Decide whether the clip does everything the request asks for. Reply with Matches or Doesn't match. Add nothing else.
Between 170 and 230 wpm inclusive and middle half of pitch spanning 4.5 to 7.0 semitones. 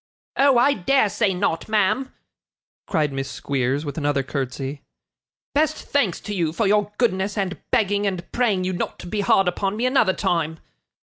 Matches